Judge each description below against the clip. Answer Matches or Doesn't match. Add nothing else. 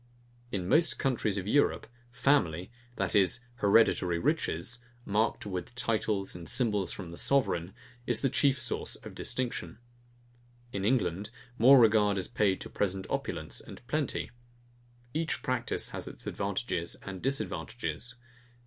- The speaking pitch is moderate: Doesn't match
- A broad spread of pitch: Doesn't match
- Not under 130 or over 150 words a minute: Matches